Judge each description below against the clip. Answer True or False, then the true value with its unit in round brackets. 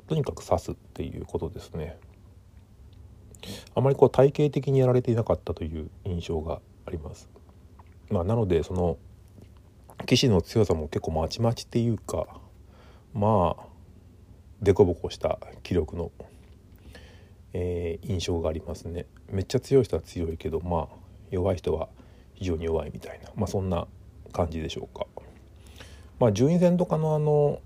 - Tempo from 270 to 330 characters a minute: True (295 characters per minute)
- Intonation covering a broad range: False (3.4 semitones)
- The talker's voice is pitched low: True (95 Hz)